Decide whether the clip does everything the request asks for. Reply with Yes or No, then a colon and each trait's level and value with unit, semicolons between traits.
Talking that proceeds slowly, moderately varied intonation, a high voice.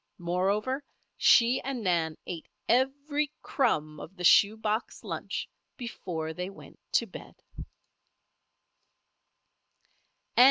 No: slow, 95 wpm; wide, 6.9 semitones; high, 205 Hz